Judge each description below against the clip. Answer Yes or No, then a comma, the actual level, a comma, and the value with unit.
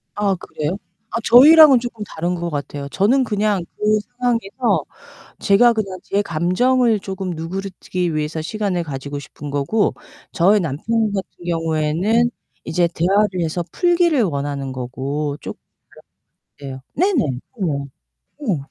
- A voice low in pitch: No, medium, 185 Hz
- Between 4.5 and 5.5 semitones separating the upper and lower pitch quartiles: No, wide, 6.0 semitones